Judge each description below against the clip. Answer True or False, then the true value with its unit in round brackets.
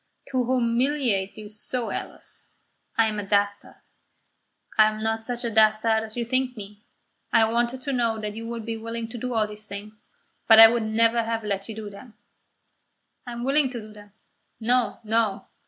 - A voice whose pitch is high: True (225 Hz)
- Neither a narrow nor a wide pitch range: False (2.0 semitones)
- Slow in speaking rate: False (190 wpm)